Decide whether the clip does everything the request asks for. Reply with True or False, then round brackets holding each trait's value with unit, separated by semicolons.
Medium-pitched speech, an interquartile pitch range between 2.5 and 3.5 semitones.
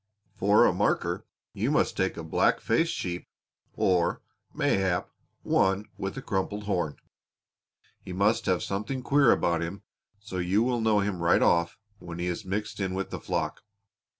False (95 Hz; 3.1 semitones)